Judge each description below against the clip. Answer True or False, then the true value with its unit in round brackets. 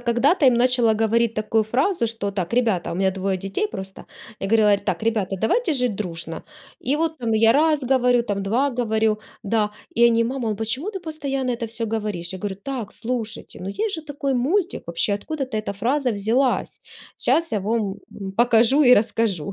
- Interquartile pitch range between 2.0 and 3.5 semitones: False (4.2 semitones)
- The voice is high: True (230 Hz)